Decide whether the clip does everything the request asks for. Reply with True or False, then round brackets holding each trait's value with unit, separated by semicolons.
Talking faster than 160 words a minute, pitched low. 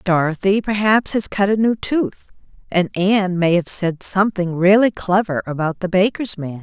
False (170 wpm; 190 Hz)